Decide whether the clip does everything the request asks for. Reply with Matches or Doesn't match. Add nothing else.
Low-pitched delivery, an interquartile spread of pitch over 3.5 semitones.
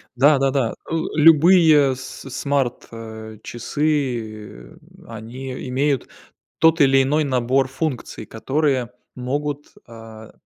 Matches